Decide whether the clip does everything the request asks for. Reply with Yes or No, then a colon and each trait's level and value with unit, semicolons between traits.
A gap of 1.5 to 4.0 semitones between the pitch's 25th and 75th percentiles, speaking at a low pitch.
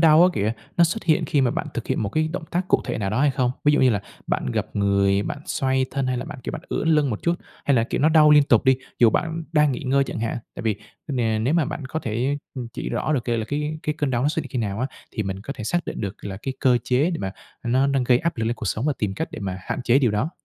No: average, 5.0 semitones; low, 130 Hz